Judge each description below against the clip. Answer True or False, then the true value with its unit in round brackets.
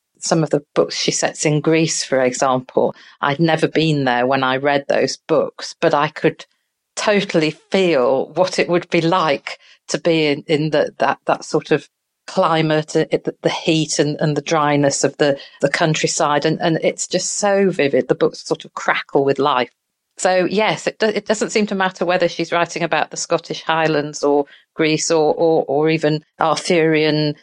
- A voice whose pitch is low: False (160 Hz)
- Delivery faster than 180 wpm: True (190 wpm)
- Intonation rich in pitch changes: False (2.8 semitones)